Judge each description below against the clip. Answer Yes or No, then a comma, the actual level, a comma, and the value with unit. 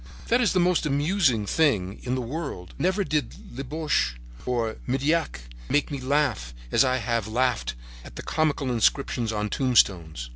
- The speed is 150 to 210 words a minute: Yes, average, 155 wpm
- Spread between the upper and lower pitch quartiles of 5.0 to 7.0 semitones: Yes, wide, 5.5 semitones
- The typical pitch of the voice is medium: No, low, 130 Hz